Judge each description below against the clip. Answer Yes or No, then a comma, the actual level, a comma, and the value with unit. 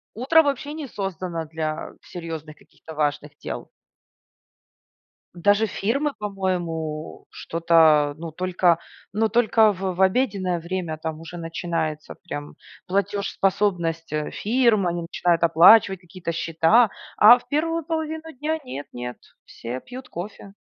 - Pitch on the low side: No, medium, 180 Hz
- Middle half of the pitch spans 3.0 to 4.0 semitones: No, average, 5.3 semitones